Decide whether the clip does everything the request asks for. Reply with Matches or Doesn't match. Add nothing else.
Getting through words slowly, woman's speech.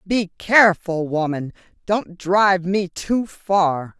Matches